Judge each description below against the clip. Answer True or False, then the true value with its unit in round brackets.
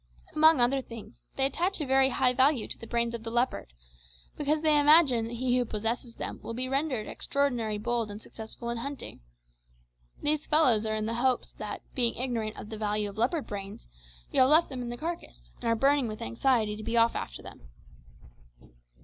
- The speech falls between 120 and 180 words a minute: False (200 wpm)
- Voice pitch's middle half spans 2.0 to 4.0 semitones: True (3.6 semitones)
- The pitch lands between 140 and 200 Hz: False (240 Hz)